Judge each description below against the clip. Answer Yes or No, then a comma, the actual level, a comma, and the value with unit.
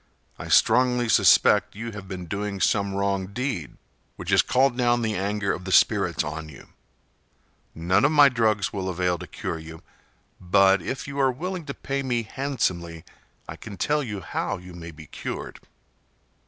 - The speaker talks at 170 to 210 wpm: Yes, average, 175 wpm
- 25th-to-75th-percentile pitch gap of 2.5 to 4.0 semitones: No, wide, 5.6 semitones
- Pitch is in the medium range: No, low, 100 Hz